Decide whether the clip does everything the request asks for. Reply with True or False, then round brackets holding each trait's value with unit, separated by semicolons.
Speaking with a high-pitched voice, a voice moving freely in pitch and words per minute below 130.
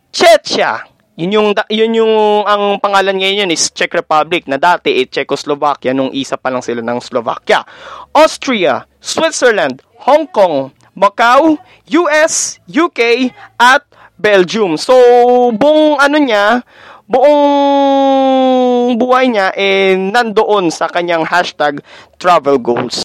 True (210 Hz; 7.7 semitones; 120 wpm)